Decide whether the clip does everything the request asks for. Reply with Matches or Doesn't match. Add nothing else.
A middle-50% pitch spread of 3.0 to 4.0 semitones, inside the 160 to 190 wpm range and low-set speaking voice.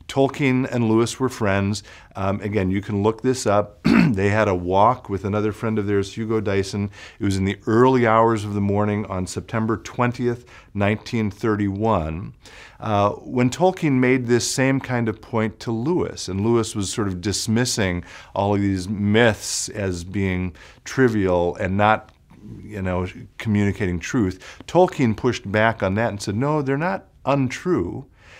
Matches